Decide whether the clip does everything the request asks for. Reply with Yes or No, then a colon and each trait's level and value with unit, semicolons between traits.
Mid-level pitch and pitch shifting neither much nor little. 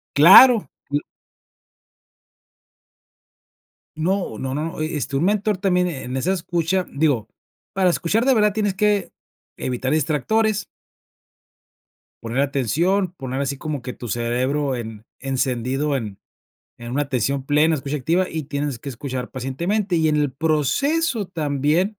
No: medium, 150 Hz; wide, 5.8 semitones